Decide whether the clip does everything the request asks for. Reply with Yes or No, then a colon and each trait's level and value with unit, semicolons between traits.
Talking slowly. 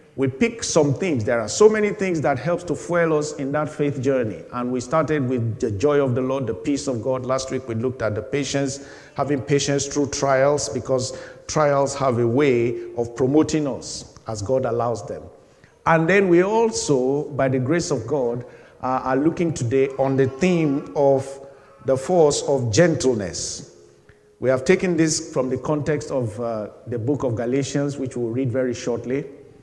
No: average, 190 wpm